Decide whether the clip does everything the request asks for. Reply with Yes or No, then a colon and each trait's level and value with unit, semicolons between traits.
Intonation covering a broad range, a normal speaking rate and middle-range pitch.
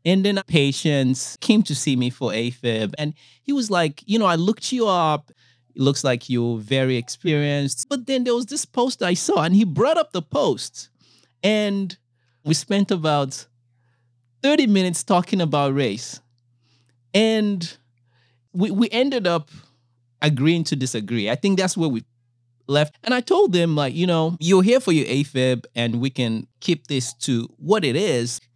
Yes: wide, 7.8 semitones; average, 175 wpm; medium, 145 Hz